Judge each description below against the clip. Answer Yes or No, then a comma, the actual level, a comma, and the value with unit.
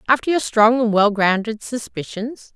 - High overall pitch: Yes, high, 225 Hz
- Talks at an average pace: Yes, average, 165 wpm